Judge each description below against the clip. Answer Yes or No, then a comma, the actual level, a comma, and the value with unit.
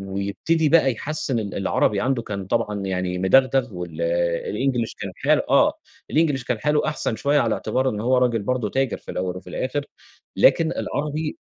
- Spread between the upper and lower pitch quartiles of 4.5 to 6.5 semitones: Yes, wide, 5.6 semitones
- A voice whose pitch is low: Yes, low, 115 Hz